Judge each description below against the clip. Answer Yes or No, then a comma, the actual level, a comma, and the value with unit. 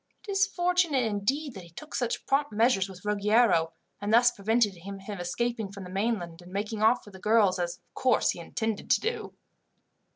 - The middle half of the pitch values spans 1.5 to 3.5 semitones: No, average, 4.1 semitones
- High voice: Yes, high, 210 Hz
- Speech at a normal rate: Yes, average, 195 wpm